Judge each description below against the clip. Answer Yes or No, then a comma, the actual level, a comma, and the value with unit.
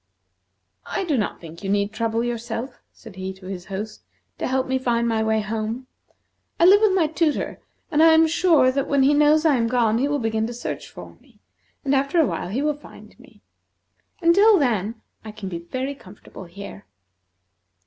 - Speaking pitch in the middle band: No, high, 240 Hz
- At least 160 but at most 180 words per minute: No, average, 200 wpm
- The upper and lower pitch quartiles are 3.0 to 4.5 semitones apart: No, wide, 5.4 semitones